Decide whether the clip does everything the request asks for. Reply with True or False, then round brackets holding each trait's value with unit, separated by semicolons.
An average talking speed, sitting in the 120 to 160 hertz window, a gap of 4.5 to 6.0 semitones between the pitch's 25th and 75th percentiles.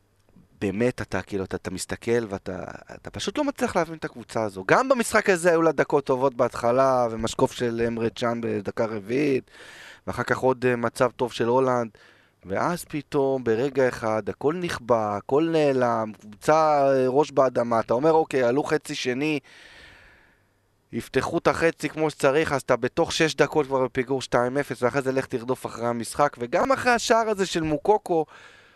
True (165 wpm; 130 Hz; 4.8 semitones)